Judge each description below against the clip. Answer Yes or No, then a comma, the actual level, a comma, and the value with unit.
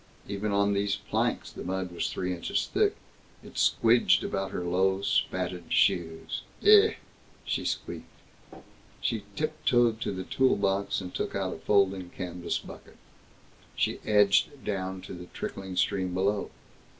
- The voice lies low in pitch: Yes, very low, 95 Hz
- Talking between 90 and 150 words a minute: Yes, average, 145 wpm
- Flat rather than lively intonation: Yes, narrow, 1.9 semitones